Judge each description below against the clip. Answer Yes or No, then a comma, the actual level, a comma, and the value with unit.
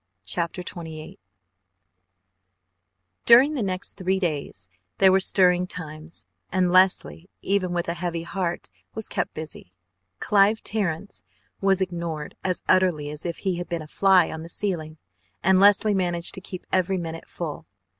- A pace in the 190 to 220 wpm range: No, average, 150 wpm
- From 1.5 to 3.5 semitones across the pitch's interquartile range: Yes, narrow, 2.6 semitones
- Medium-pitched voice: Yes, medium, 180 Hz